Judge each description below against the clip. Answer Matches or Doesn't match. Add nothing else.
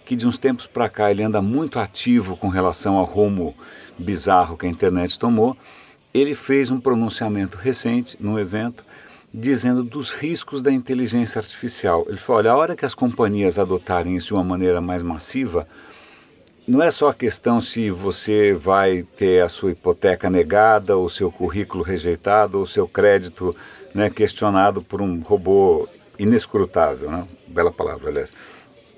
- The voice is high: Doesn't match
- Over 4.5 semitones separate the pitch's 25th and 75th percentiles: Matches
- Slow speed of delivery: Doesn't match